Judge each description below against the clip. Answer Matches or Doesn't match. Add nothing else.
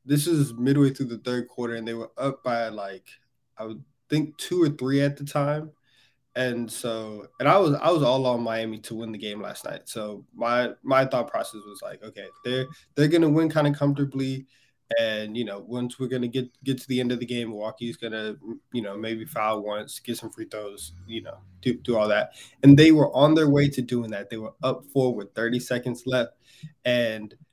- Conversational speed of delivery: Doesn't match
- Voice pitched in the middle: Doesn't match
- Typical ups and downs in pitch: Matches